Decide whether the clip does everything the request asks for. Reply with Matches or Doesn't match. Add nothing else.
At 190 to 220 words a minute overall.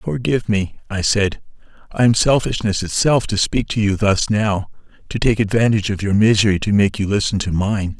Matches